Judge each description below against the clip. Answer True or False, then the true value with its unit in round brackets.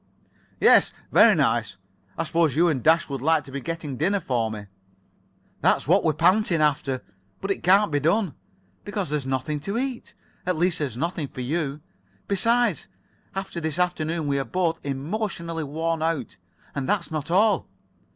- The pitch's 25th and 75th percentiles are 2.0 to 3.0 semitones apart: False (4.4 semitones)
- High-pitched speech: False (160 Hz)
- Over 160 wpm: True (170 wpm)